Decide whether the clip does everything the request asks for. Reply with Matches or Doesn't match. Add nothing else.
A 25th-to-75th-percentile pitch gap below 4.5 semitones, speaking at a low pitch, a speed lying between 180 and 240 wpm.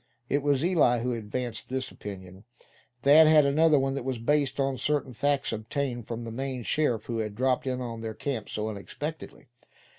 Matches